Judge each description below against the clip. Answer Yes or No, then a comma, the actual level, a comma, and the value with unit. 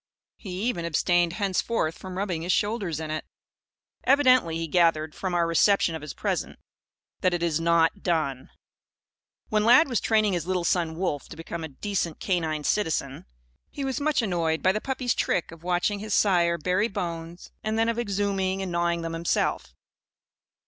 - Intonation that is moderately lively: Yes, average, 3.8 semitones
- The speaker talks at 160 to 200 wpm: Yes, average, 175 wpm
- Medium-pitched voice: Yes, medium, 175 Hz